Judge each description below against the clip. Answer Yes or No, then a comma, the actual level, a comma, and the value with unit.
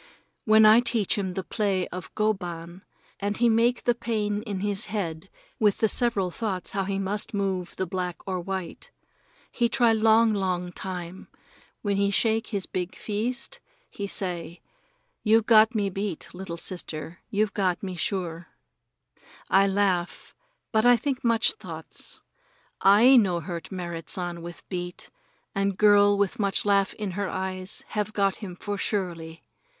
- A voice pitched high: Yes, high, 195 Hz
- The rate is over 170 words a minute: No, average, 160 wpm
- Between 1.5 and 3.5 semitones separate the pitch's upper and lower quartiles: Yes, average, 3.0 semitones